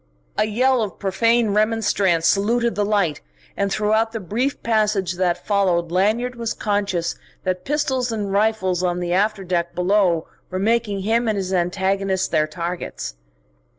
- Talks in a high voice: Yes, high, 200 Hz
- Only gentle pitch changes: No, average, 3.4 semitones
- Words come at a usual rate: Yes, average, 150 wpm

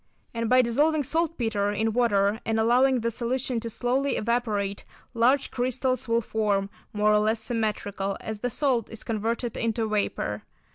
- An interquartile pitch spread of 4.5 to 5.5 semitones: No, average, 2.8 semitones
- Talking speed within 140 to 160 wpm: Yes, average, 155 wpm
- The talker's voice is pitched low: No, high, 230 Hz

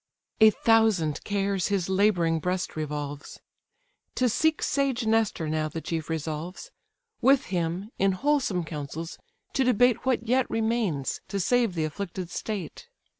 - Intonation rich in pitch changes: Yes, wide, 5.8 semitones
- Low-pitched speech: No, high, 195 Hz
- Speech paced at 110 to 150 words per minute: Yes, slow, 135 wpm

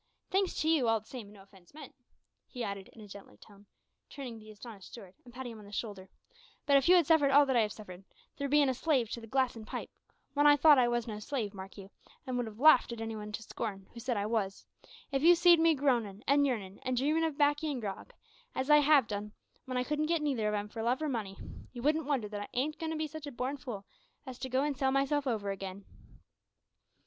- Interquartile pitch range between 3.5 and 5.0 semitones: No, wide, 5.4 semitones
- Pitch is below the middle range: No, high, 245 Hz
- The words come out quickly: Yes, fast, 260 wpm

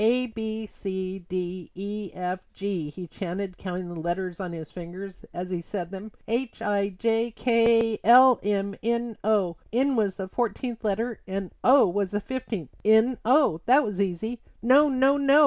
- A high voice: Yes, high, 205 Hz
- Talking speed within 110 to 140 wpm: No, average, 175 wpm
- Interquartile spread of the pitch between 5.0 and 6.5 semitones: No, average, 4.0 semitones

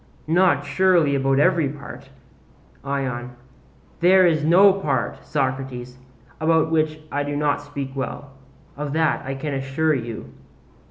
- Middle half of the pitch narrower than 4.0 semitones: Yes, average, 3.0 semitones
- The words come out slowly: Yes, slow, 130 wpm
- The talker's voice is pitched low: No, medium, 145 Hz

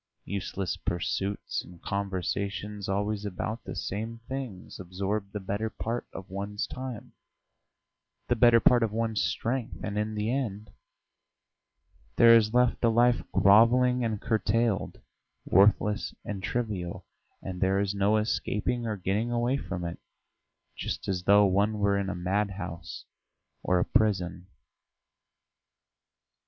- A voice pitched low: Yes, low, 105 Hz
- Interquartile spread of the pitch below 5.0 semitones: Yes, average, 2.9 semitones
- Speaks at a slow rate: Yes, slow, 130 wpm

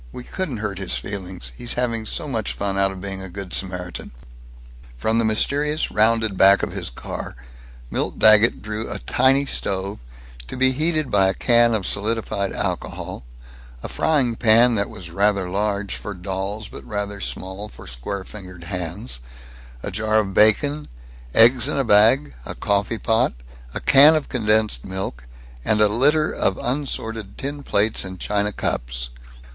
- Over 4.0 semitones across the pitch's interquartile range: No, average, 3.5 semitones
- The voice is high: No, low, 105 Hz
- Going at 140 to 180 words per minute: Yes, average, 165 wpm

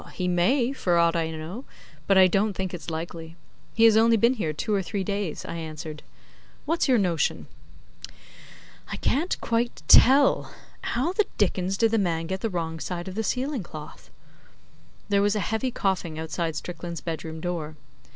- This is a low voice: No, medium, 185 Hz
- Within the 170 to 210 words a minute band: Yes, average, 175 wpm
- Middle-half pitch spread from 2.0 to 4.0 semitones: No, average, 5.3 semitones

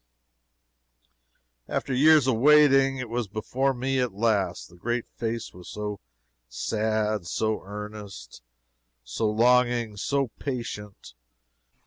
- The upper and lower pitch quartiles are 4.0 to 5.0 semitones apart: No, average, 3.5 semitones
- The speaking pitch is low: Yes, low, 115 Hz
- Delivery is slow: Yes, slow, 110 wpm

